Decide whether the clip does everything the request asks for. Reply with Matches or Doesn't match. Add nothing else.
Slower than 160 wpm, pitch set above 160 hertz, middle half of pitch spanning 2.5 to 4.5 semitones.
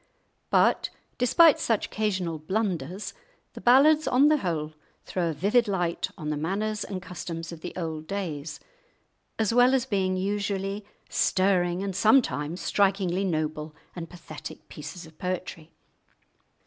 Matches